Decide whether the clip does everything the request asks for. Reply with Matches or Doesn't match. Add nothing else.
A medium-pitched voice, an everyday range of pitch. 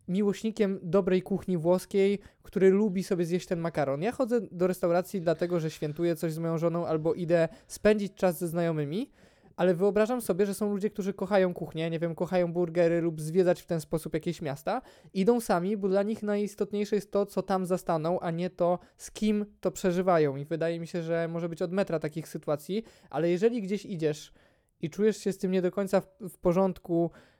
Matches